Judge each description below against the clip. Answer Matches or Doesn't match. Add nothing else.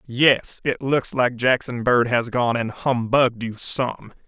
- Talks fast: Doesn't match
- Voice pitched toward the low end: Matches